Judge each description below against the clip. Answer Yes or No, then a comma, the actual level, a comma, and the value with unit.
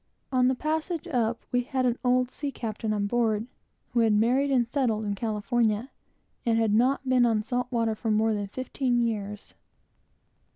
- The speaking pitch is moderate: No, high, 235 Hz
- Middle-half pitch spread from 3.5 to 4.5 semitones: No, average, 2.8 semitones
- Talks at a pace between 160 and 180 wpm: Yes, average, 175 wpm